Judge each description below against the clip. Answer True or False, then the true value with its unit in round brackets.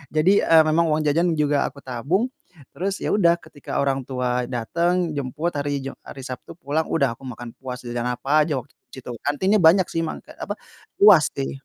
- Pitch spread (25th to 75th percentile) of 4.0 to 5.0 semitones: True (4.4 semitones)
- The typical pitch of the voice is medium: True (145 Hz)